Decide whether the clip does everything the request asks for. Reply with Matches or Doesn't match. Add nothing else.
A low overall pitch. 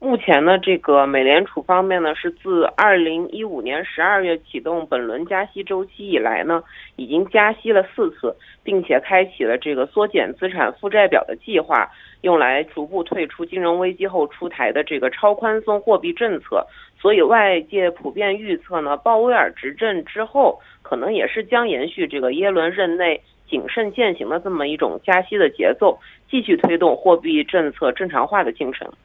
Doesn't match